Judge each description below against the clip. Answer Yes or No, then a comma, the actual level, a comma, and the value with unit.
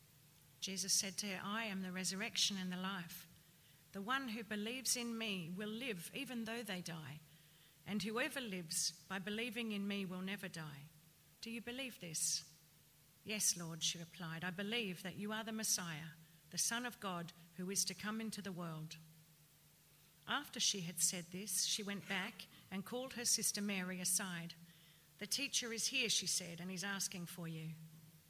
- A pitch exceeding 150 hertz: Yes, medium, 185 Hz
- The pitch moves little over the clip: No, average, 4.4 semitones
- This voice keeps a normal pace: Yes, average, 180 wpm